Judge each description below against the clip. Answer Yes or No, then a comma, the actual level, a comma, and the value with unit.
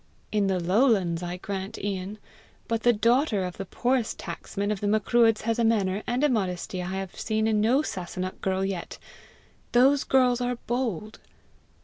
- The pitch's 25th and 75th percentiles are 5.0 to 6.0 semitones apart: No, average, 4.1 semitones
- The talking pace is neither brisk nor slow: Yes, average, 170 wpm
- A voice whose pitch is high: Yes, high, 210 Hz